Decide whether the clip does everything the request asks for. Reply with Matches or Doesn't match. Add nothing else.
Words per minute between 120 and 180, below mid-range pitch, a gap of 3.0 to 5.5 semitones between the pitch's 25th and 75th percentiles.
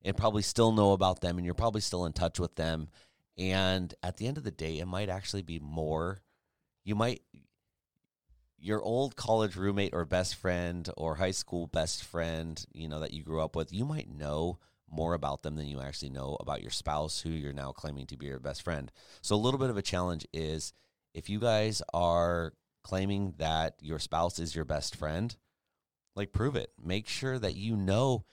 Doesn't match